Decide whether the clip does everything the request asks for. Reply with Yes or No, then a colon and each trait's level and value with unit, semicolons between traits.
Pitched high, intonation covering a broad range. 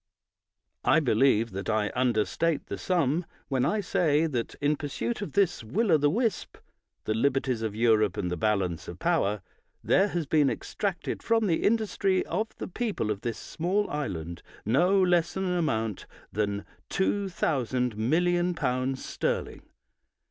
No: medium, 145 Hz; wide, 8.4 semitones